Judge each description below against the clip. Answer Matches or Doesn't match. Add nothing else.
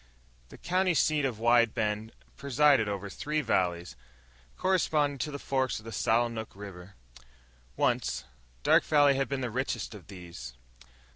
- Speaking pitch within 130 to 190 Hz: Doesn't match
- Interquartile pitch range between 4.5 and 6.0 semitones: Matches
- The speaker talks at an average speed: Matches